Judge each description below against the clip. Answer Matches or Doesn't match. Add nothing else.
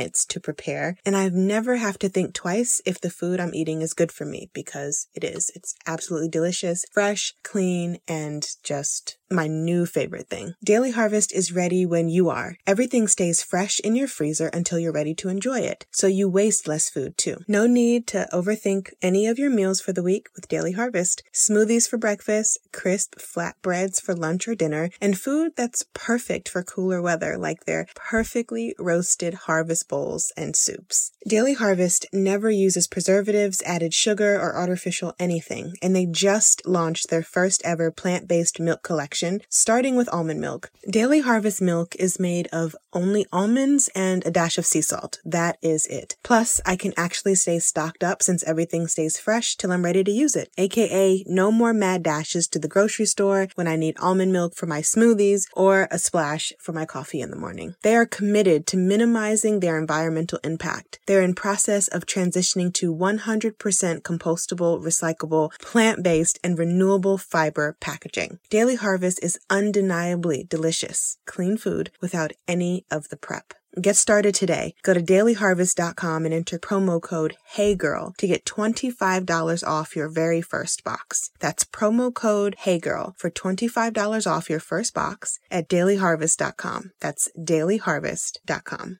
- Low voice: Doesn't match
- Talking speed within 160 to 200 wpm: Matches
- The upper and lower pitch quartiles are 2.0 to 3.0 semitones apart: Doesn't match